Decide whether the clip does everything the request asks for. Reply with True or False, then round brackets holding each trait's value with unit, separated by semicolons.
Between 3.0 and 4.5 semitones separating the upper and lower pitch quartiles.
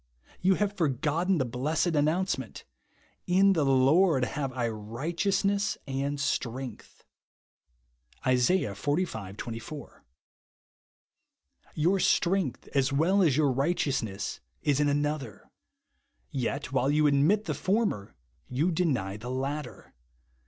False (5.3 semitones)